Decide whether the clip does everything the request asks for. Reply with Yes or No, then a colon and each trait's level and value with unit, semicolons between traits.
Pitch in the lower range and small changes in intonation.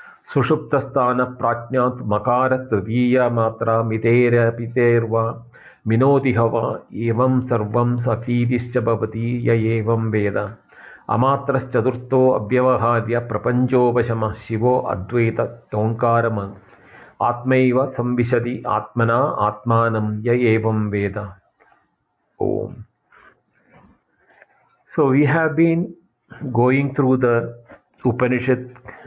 Yes: low, 120 Hz; narrow, 1.9 semitones